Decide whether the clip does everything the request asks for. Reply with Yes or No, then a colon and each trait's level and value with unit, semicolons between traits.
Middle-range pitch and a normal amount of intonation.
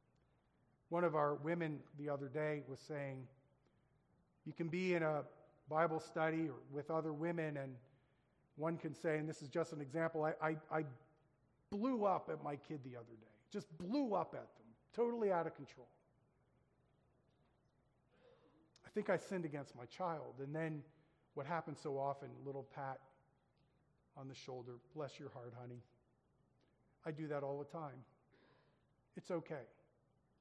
Yes: medium, 145 Hz; average, 3.1 semitones